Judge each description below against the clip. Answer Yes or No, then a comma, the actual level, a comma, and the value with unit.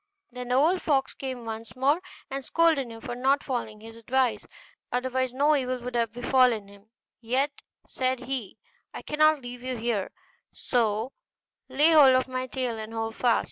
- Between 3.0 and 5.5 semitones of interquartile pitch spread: No, narrow, 2.6 semitones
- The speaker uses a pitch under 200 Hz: No, very high, 255 Hz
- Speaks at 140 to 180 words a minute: Yes, average, 175 wpm